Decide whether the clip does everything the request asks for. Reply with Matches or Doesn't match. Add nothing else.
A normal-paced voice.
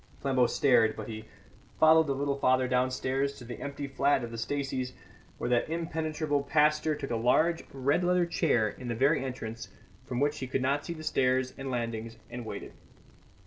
Matches